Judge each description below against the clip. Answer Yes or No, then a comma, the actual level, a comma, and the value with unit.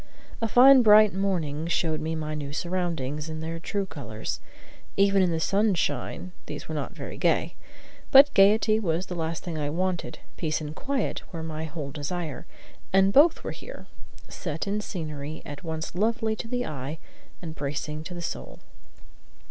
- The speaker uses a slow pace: No, average, 170 wpm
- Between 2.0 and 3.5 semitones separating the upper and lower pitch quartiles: No, average, 4.3 semitones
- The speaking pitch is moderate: Yes, medium, 170 Hz